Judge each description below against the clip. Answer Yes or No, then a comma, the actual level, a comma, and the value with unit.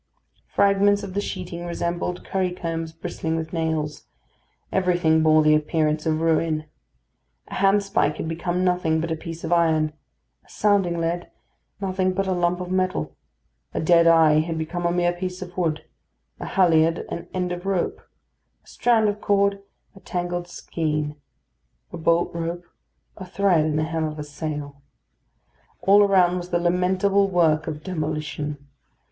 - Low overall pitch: No, medium, 170 Hz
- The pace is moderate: Yes, average, 155 wpm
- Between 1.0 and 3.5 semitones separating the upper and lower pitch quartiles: Yes, narrow, 2.5 semitones